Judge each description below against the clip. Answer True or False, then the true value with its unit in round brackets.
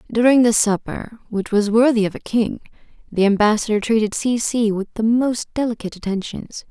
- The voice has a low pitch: False (220 Hz)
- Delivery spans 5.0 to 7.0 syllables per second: True (5.4 syllables/s)